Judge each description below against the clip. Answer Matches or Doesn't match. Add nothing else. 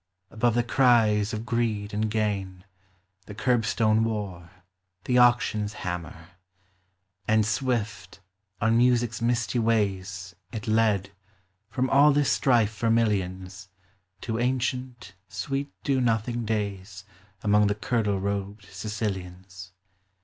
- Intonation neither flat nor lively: Matches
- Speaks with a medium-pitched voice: Doesn't match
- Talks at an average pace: Doesn't match